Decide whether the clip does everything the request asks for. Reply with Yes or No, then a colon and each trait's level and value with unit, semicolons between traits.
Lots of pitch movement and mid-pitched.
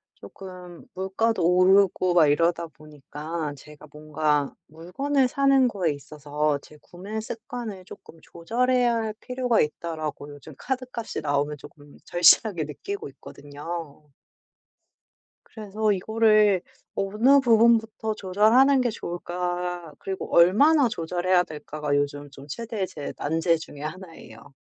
Yes: wide, 6.4 semitones; medium, 180 Hz